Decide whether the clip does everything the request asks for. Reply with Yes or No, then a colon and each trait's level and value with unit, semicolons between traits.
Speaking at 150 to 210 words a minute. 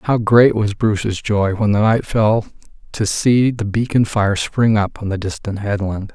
Yes: average, 195 wpm